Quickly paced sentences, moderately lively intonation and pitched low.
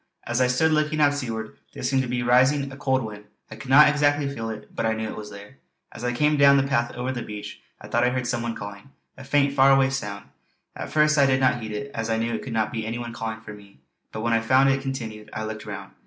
Yes: fast, 280 wpm; average, 3.7 semitones; low, 120 Hz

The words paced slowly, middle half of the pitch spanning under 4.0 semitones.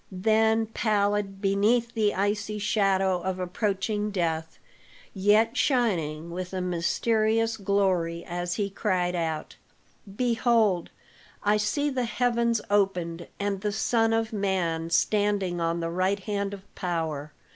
Yes: slow, 125 wpm; average, 3.5 semitones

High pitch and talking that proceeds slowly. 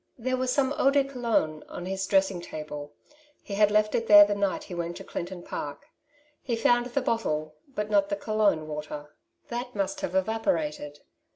No: high, 200 Hz; average, 185 wpm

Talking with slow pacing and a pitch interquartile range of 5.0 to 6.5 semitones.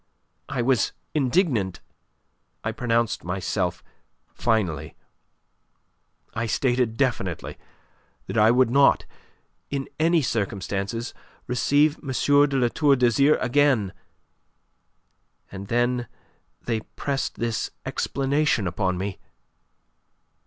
Yes: slow, 95 wpm; average, 5.3 semitones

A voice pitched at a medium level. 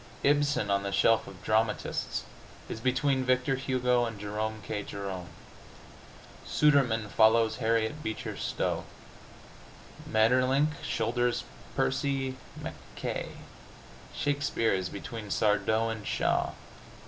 No: low, 115 Hz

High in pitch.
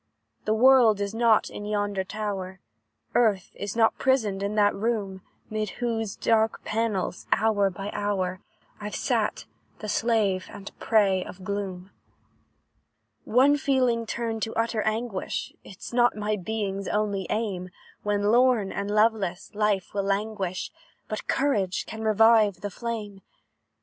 Yes: high, 210 Hz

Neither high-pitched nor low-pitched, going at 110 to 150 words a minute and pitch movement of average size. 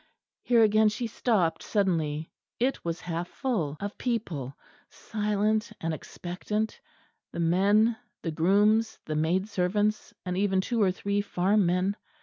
No: high, 200 Hz; slow, 135 wpm; average, 3.7 semitones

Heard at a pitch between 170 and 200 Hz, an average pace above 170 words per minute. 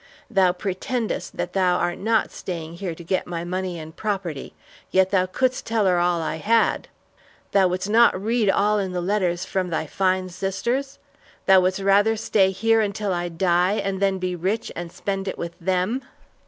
Yes: high, 190 Hz; average, 185 wpm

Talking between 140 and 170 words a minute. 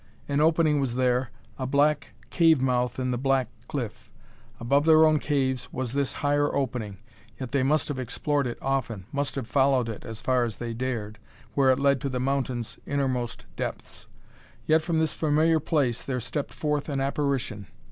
No: average, 180 wpm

